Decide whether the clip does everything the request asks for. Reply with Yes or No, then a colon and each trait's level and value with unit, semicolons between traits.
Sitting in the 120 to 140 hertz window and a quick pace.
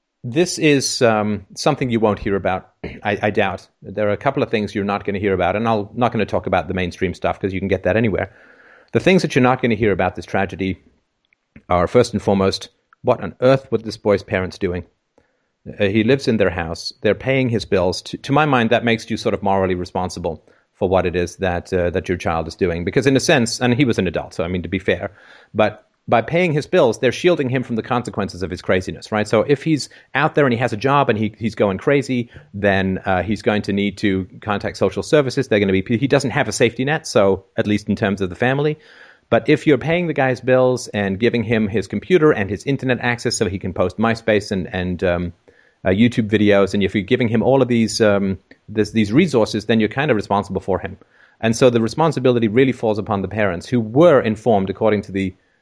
No: low, 110 Hz; fast, 255 wpm